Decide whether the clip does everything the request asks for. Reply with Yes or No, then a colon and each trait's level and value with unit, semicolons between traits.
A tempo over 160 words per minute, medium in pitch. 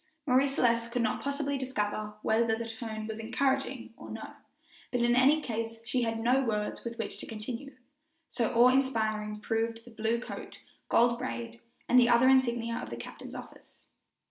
No: average, 175 wpm; high, 235 Hz